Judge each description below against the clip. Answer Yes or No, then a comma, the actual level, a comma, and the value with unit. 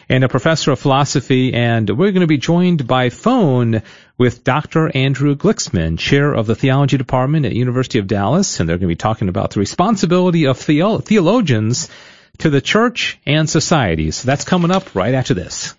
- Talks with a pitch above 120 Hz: Yes, medium, 140 Hz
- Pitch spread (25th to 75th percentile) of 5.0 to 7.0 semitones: Yes, wide, 5.5 semitones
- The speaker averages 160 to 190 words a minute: Yes, average, 185 wpm